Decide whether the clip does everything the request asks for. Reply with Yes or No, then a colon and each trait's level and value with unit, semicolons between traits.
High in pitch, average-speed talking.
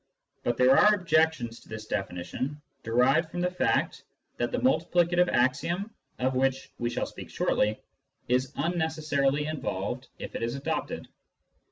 No: low, 135 Hz; average, 150 wpm